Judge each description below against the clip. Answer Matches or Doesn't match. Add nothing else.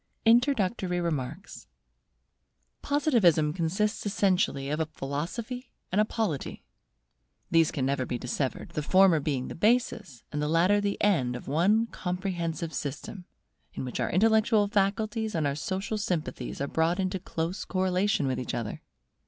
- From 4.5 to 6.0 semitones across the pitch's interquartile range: Matches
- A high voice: Doesn't match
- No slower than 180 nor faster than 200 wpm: Doesn't match